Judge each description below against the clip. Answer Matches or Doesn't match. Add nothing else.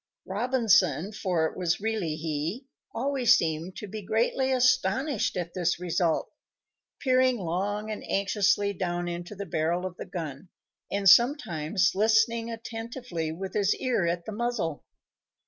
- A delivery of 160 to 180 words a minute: Doesn't match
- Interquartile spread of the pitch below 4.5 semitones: Doesn't match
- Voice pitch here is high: Matches